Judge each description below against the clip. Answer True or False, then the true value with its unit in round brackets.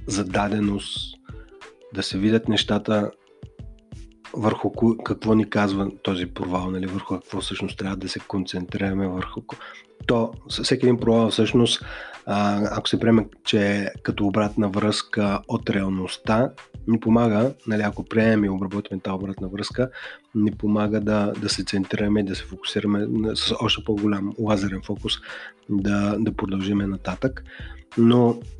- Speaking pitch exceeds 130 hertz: False (105 Hz)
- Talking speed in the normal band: True (140 wpm)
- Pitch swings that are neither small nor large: False (2.0 semitones)